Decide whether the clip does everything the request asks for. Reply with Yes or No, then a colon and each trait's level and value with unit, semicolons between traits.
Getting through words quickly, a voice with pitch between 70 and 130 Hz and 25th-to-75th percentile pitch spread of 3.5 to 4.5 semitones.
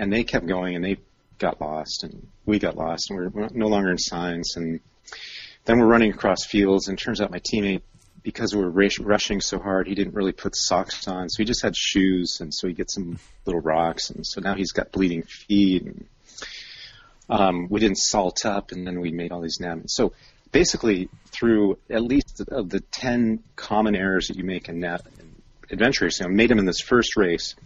No: fast, 220 wpm; very low, 95 Hz; average, 3.1 semitones